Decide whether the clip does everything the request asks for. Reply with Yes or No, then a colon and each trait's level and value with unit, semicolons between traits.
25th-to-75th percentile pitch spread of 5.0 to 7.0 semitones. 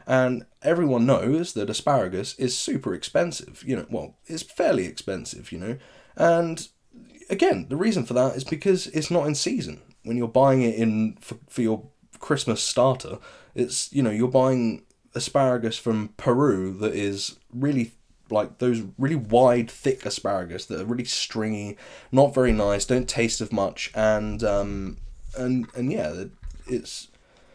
No: average, 3.4 semitones